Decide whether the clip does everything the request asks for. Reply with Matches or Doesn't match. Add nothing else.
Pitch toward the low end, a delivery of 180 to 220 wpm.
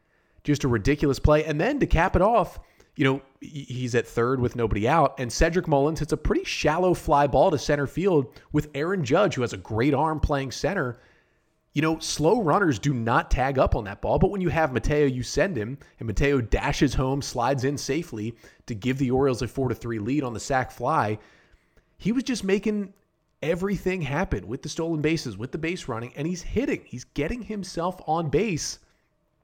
Doesn't match